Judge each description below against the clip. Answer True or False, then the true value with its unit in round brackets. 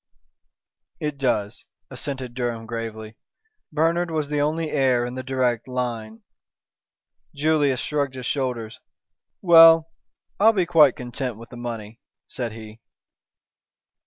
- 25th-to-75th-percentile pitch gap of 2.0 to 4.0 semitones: False (4.4 semitones)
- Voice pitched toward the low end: True (130 Hz)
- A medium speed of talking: False (120 wpm)